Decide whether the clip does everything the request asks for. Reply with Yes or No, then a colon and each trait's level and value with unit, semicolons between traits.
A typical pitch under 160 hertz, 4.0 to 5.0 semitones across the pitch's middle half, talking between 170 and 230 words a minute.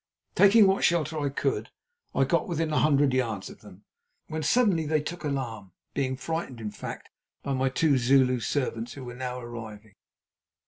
Yes: low, 135 Hz; average, 4.4 semitones; average, 175 wpm